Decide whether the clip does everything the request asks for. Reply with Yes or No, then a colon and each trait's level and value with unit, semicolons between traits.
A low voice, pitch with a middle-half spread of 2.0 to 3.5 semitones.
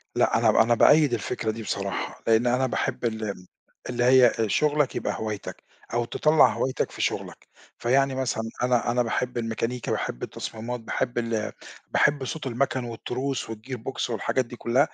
Yes: low, 120 Hz; narrow, 2.4 semitones